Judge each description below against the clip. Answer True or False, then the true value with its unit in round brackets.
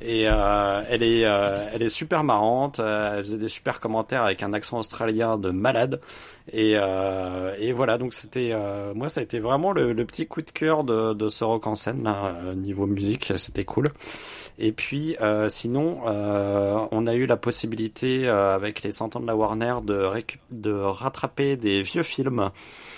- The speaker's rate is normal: True (190 wpm)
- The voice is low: True (110 Hz)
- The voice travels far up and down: False (2.9 semitones)